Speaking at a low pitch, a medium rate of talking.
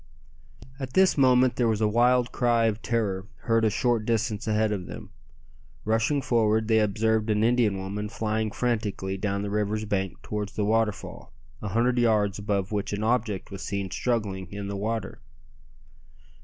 Yes: low, 110 Hz; average, 170 wpm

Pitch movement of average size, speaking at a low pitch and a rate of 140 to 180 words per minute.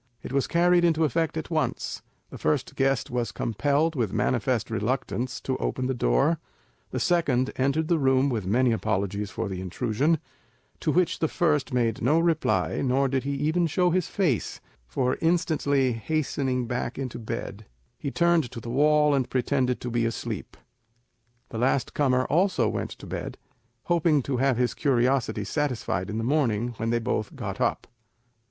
Yes: average, 4.6 semitones; low, 130 Hz; average, 170 wpm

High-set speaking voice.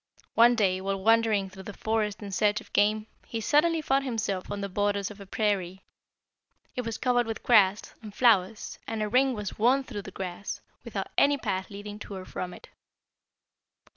Yes: high, 210 Hz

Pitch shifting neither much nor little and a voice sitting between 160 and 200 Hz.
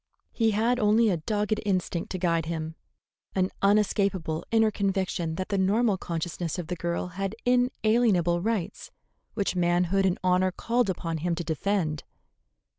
Yes: average, 3.5 semitones; medium, 185 Hz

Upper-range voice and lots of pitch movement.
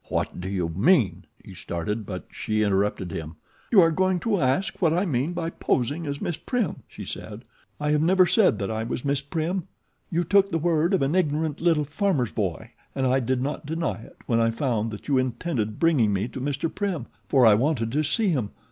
No: medium, 140 Hz; wide, 6.9 semitones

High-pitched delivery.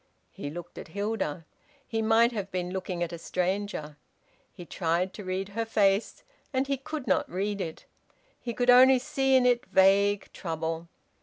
Yes: high, 195 Hz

